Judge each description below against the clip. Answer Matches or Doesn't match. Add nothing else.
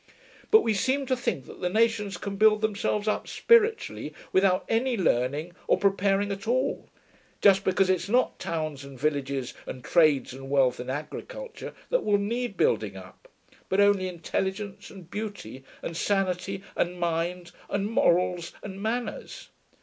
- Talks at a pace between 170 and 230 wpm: Doesn't match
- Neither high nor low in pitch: Doesn't match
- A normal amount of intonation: Matches